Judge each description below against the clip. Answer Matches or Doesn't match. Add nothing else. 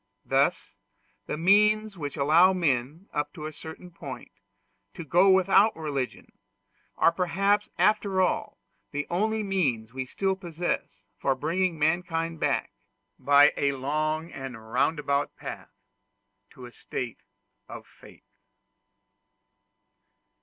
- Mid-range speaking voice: Matches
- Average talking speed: Doesn't match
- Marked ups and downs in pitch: Doesn't match